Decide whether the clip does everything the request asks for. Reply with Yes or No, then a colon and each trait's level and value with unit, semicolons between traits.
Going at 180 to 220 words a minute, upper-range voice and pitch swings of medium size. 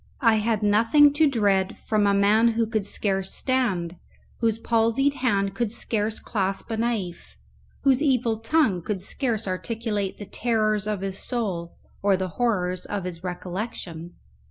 No: average, 155 wpm; high, 215 Hz; average, 3.3 semitones